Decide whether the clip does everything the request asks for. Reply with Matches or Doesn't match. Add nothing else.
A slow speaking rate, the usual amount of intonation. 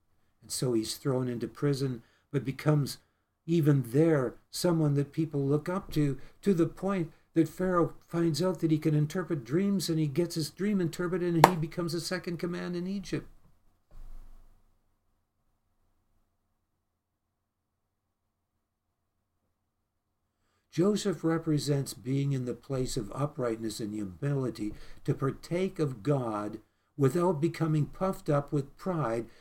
Doesn't match